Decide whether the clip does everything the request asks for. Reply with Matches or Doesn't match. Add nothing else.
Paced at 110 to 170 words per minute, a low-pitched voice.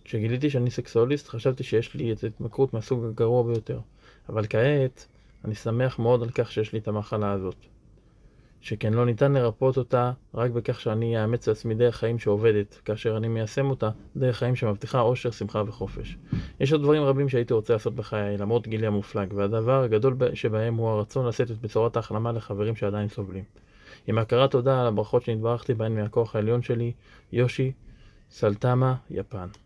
Matches